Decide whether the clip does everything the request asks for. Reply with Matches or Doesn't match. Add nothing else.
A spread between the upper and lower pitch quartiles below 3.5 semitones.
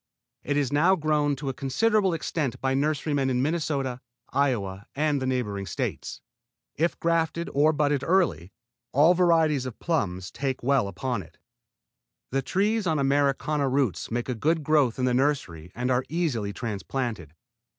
Doesn't match